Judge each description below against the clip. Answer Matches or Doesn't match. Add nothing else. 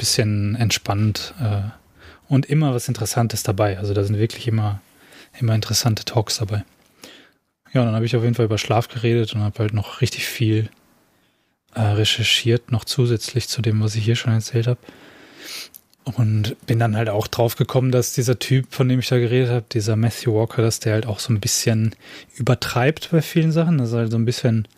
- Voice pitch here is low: Matches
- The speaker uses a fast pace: Matches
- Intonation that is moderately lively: Doesn't match